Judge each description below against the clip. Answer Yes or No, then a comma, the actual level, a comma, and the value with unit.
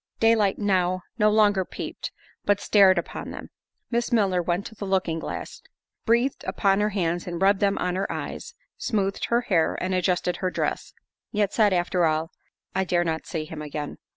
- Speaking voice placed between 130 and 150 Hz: No, high, 190 Hz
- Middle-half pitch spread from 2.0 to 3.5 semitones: Yes, average, 2.9 semitones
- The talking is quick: No, average, 180 wpm